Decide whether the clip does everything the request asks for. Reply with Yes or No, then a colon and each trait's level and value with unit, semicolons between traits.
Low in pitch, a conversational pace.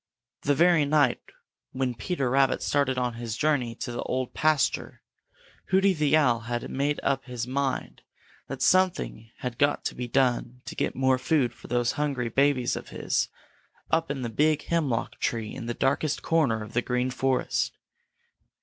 Yes: low, 130 Hz; average, 170 wpm